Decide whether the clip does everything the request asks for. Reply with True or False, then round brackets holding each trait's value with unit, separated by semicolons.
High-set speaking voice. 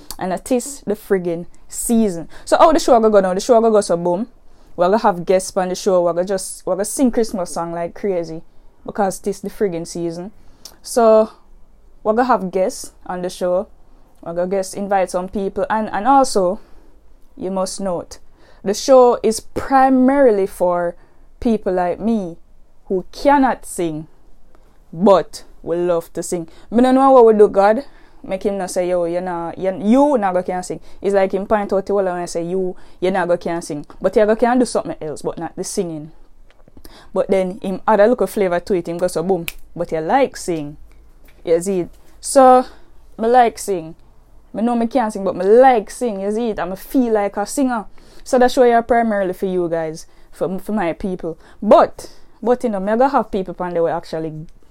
True (195 Hz)